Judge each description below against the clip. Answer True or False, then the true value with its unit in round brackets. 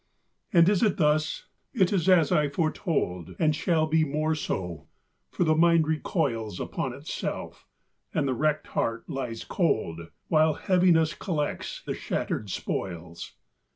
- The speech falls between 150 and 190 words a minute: False (140 wpm)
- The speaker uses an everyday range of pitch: False (5.7 semitones)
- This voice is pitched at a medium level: True (155 Hz)